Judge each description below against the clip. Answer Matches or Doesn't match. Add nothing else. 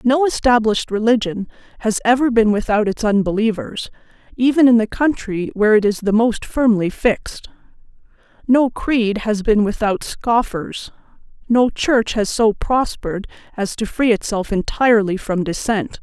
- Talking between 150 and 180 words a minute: Doesn't match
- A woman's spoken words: Matches